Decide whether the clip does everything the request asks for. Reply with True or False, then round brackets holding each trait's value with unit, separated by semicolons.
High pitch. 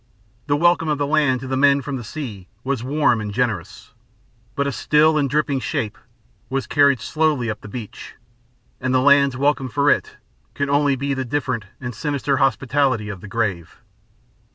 False (135 Hz)